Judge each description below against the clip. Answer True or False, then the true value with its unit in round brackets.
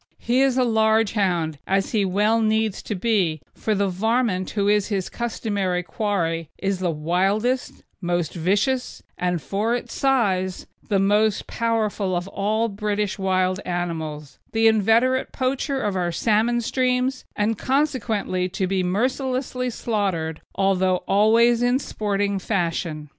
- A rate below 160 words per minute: True (140 wpm)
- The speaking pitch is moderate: False (205 Hz)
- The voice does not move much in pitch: False (3.8 semitones)